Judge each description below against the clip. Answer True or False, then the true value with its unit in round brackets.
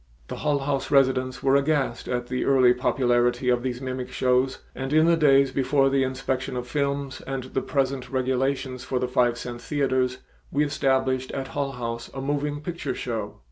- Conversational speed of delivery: True (180 wpm)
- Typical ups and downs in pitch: False (1.6 semitones)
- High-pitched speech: False (130 Hz)